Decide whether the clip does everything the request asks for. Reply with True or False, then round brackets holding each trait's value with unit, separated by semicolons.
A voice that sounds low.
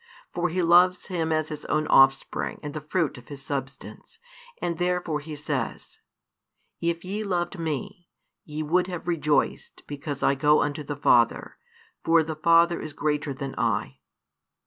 False (155 Hz)